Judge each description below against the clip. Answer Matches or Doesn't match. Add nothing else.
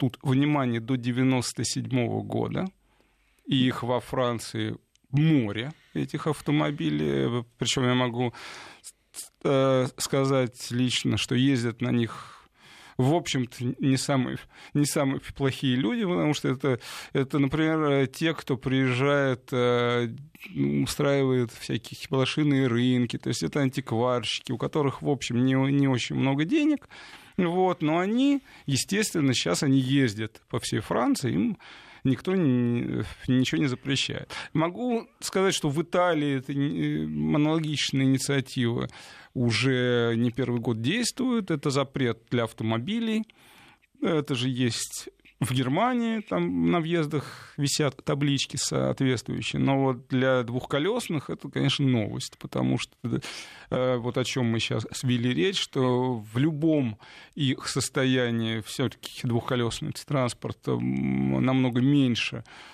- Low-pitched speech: Matches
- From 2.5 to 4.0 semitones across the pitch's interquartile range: Matches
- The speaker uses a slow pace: Doesn't match